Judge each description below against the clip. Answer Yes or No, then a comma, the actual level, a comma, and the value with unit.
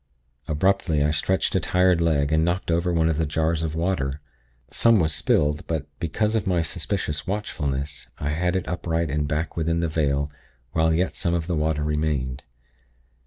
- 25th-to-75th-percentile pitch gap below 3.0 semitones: Yes, narrow, 2.6 semitones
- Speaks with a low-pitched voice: Yes, very low, 80 Hz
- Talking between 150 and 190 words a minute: Yes, average, 180 wpm